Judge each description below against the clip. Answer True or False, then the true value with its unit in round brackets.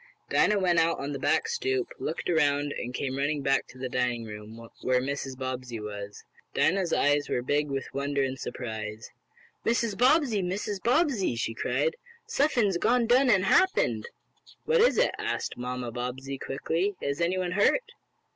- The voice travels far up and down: True (8.5 semitones)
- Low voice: False (145 Hz)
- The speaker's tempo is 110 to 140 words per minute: False (165 wpm)